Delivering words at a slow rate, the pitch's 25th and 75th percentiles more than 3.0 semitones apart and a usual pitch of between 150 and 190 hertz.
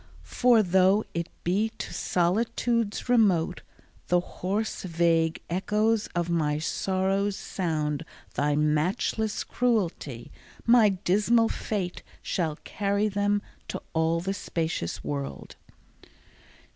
Yes: slow, 105 wpm; average, 4.2 semitones; medium, 185 Hz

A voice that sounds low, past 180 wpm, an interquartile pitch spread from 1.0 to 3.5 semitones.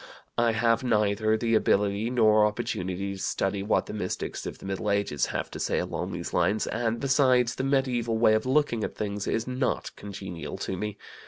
Yes: low, 110 Hz; average, 190 wpm; average, 2.9 semitones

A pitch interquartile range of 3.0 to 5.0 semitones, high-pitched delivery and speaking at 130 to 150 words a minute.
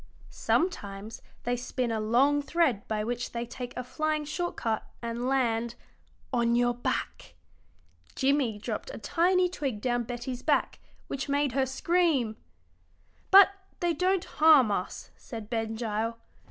Yes: average, 4.4 semitones; high, 245 Hz; average, 140 wpm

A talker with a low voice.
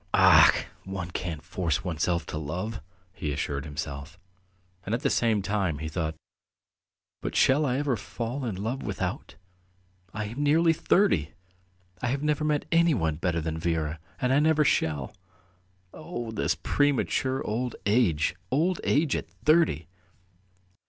Yes: low, 105 Hz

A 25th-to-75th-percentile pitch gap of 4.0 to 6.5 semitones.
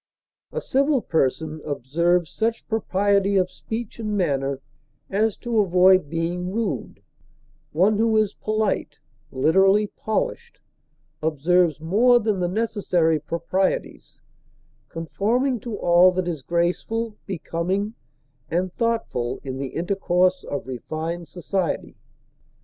Yes: average, 4.6 semitones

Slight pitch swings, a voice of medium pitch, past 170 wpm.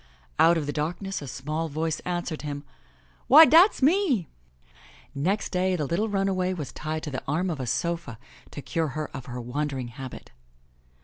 No: average, 4.6 semitones; medium, 155 Hz; average, 185 wpm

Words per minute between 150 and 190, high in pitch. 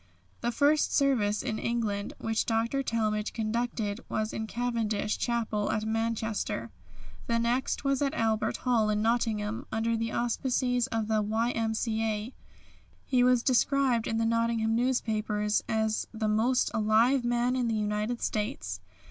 No: average, 140 wpm; high, 225 Hz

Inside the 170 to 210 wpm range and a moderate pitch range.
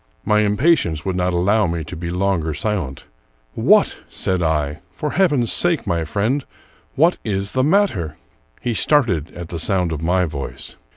No: average, 180 wpm; wide, 6.1 semitones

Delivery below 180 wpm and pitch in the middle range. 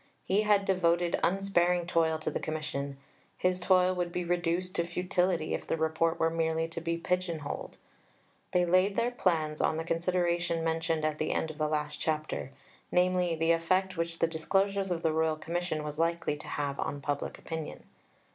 No: average, 185 wpm; medium, 170 Hz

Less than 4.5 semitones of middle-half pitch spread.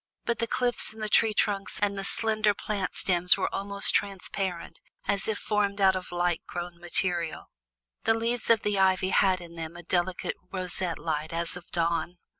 Yes: average, 2.9 semitones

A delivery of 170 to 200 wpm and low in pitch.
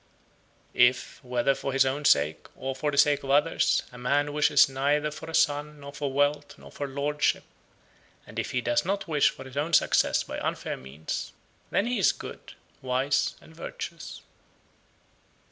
No: average, 180 wpm; medium, 145 Hz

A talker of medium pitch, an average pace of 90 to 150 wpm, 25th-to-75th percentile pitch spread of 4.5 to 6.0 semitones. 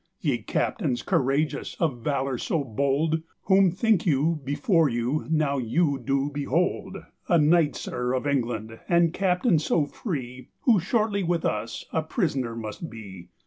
Yes: medium, 145 Hz; average, 145 wpm; average, 5.0 semitones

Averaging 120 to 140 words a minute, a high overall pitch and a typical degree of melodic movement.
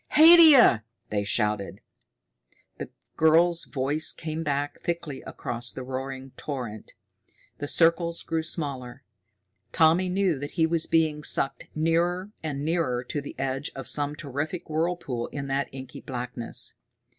No: slow, 135 wpm; medium, 145 Hz; average, 4.0 semitones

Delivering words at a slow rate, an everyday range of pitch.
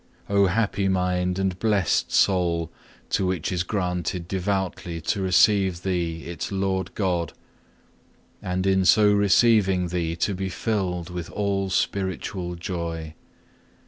No: slow, 125 wpm; narrow, 1.9 semitones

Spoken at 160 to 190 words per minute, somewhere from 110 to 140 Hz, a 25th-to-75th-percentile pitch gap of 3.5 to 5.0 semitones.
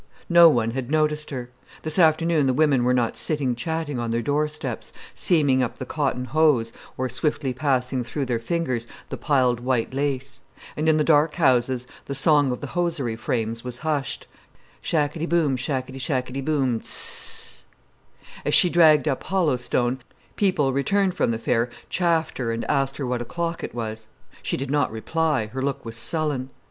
Yes: average, 180 wpm; low, 135 Hz; average, 3.8 semitones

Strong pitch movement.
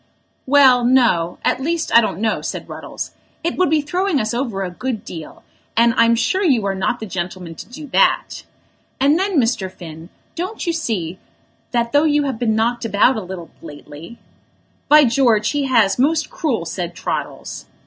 Yes: wide, 6.9 semitones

